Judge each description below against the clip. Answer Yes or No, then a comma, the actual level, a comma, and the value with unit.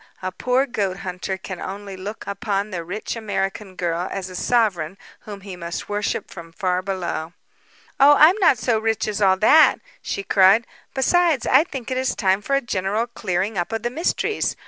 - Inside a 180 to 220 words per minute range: Yes, average, 190 wpm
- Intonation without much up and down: No, average, 4.2 semitones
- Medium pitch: No, high, 200 Hz